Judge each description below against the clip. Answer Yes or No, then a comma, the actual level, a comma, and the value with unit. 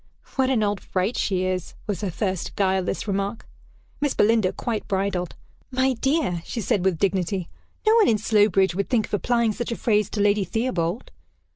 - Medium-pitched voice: No, high, 205 Hz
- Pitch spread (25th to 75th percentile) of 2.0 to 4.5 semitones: Yes, average, 3.6 semitones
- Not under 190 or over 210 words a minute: No, average, 180 wpm